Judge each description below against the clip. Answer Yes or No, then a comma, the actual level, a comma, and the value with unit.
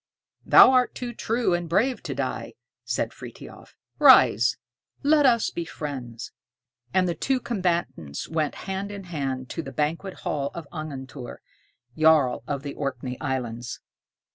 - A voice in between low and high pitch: Yes, medium, 160 Hz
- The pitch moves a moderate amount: No, wide, 6.3 semitones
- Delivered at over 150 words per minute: No, average, 145 wpm